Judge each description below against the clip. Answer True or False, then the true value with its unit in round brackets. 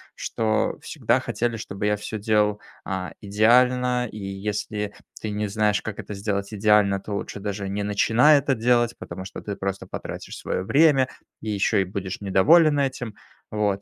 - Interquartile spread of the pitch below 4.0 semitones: True (3.0 semitones)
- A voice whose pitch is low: True (105 Hz)